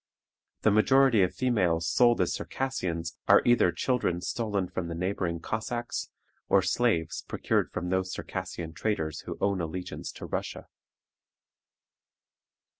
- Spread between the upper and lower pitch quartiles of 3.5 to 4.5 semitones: No, wide, 5.4 semitones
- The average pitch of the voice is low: Yes, very low, 95 Hz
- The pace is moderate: No, slow, 125 wpm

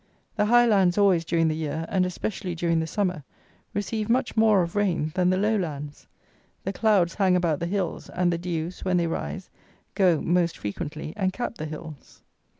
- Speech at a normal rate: Yes, average, 190 wpm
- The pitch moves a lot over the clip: No, average, 3.5 semitones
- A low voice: No, medium, 180 Hz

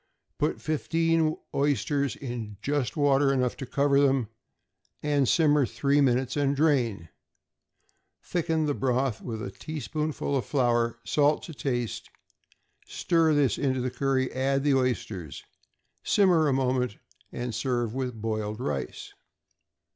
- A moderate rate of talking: No, slow, 125 wpm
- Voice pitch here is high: No, low, 135 Hz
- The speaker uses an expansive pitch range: No, average, 3.2 semitones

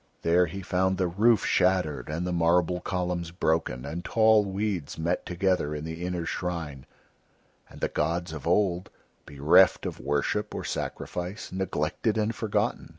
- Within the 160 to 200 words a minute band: No, average, 150 wpm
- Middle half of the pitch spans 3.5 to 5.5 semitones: No, average, 2.8 semitones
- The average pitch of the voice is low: Yes, very low, 90 Hz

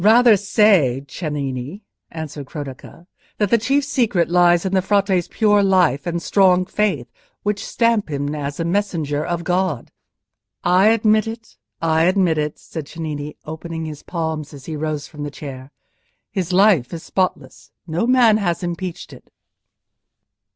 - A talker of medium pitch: Yes, medium, 175 Hz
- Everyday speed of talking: Yes, average, 150 wpm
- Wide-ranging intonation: No, average, 5.0 semitones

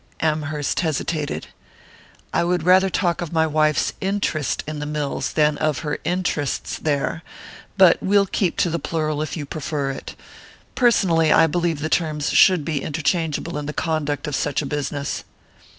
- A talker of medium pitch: Yes, medium, 155 Hz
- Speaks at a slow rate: No, average, 165 wpm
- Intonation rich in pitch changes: No, narrow, 2.5 semitones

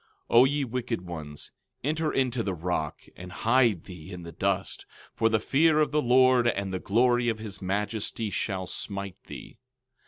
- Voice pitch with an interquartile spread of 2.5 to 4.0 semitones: No, average, 5.3 semitones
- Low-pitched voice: Yes, low, 110 Hz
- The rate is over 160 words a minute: Yes, average, 180 wpm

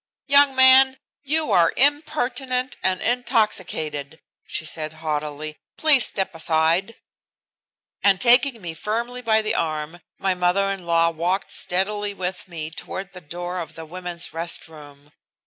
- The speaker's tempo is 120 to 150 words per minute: Yes, average, 140 wpm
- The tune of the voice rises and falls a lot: Yes, wide, 6.8 semitones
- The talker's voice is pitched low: No, medium, 185 Hz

